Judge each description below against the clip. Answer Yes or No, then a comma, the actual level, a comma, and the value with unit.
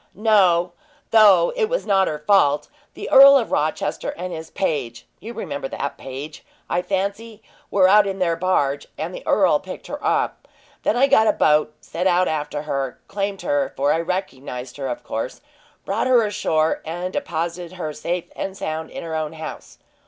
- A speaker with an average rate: Yes, average, 180 wpm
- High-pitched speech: No, medium, 175 Hz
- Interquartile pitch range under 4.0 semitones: No, average, 4.7 semitones